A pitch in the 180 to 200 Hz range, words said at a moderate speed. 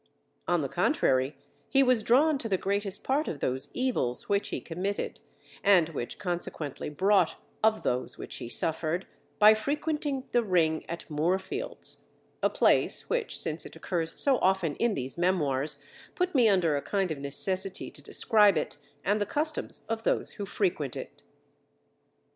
Yes: high, 190 Hz; average, 160 wpm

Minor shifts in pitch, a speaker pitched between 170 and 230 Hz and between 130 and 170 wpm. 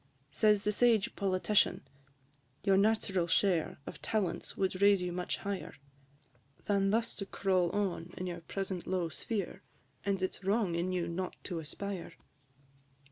Yes: narrow, 2.1 semitones; high, 190 Hz; average, 150 wpm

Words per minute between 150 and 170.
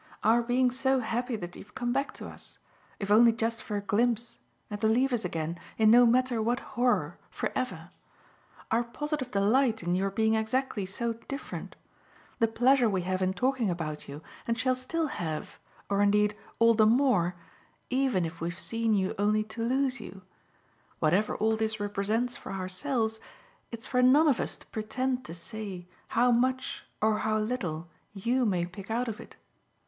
No: average, 180 wpm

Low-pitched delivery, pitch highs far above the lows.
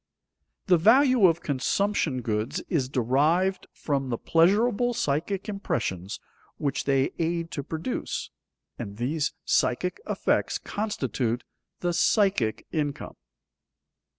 No: medium, 160 Hz; wide, 6.8 semitones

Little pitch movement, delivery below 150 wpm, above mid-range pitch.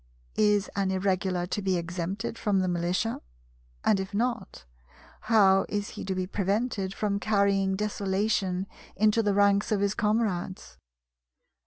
Yes: narrow, 1.8 semitones; average, 140 wpm; high, 200 Hz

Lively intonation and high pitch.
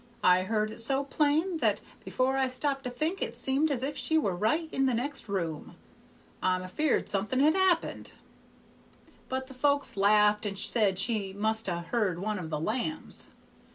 Yes: wide, 6.0 semitones; high, 235 Hz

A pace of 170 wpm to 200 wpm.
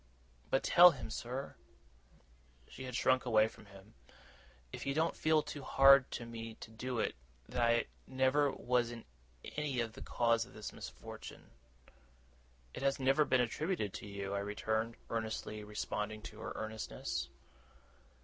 No: average, 155 wpm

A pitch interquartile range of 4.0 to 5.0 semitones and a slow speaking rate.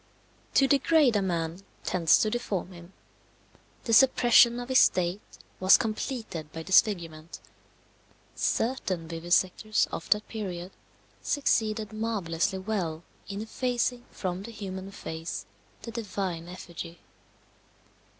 Yes: average, 4.6 semitones; slow, 110 wpm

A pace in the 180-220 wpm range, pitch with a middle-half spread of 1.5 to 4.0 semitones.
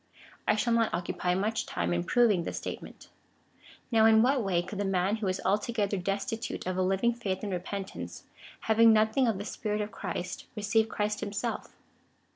Yes: average, 185 wpm; average, 2.8 semitones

